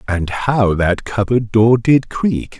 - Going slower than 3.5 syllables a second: Yes, 3.3 syllables/s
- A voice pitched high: No, low, 110 Hz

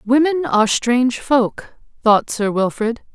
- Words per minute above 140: No, slow, 135 wpm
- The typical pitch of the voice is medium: No, high, 240 Hz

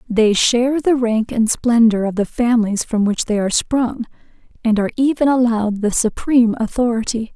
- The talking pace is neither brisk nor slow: Yes, average, 170 wpm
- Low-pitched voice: No, high, 230 Hz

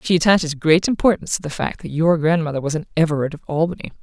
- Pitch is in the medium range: Yes, medium, 160 Hz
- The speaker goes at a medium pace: No, fast, 225 wpm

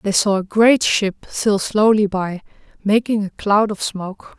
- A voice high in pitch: Yes, high, 205 Hz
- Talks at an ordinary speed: Yes, average, 180 wpm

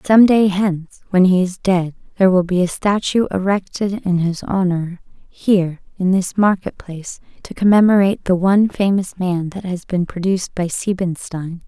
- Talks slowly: No, average, 170 wpm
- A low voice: No, medium, 185 Hz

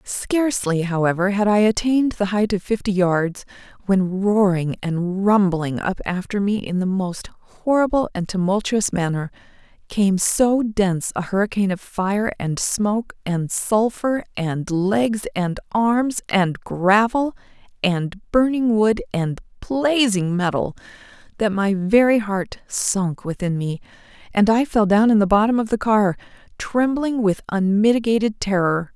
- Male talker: No, female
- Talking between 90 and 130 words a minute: No, average, 140 wpm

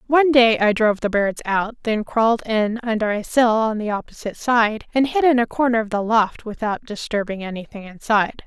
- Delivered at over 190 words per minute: Yes, fast, 205 wpm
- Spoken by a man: No, female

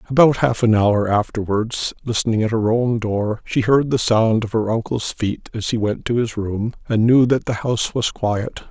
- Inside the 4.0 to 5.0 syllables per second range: Yes, 4.7 syllables/s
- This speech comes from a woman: No, male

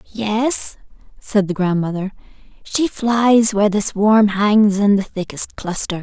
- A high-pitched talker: Yes, high, 205 Hz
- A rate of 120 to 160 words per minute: Yes, average, 140 wpm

